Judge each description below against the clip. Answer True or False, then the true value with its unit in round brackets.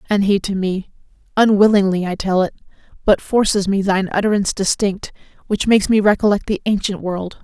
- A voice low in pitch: False (200 Hz)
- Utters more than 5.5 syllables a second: True (5.8 syllables/s)